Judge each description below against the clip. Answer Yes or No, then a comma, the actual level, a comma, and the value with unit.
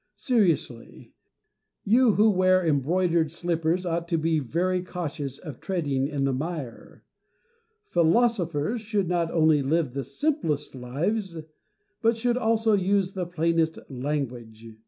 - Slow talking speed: Yes, slow, 125 wpm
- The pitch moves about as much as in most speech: Yes, average, 4.8 semitones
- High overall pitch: No, medium, 170 Hz